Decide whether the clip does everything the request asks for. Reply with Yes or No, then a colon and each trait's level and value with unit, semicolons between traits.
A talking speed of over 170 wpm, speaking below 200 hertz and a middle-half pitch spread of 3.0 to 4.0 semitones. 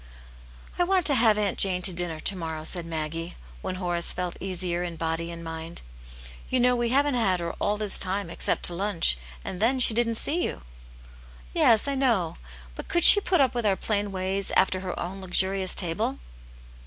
No: average, 200 wpm; high, 190 Hz; average, 5.1 semitones